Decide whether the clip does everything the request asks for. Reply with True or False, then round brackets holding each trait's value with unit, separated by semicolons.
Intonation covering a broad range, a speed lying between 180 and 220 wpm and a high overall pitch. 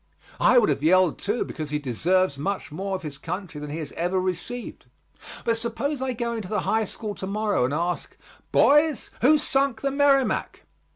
True (6.8 semitones; 190 wpm; 195 Hz)